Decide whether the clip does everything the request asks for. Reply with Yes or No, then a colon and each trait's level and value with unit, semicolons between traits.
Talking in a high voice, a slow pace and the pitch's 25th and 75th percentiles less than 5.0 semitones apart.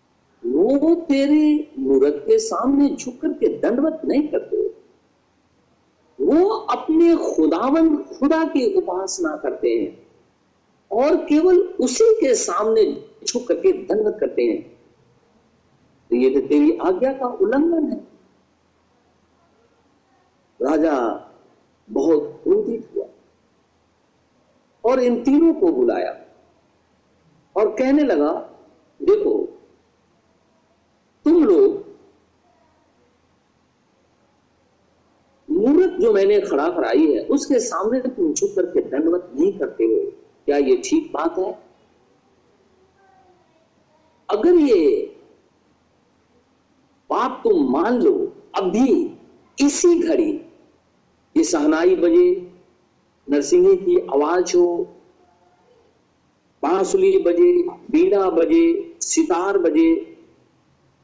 Yes: very high, 355 Hz; slow, 90 wpm; average, 4.0 semitones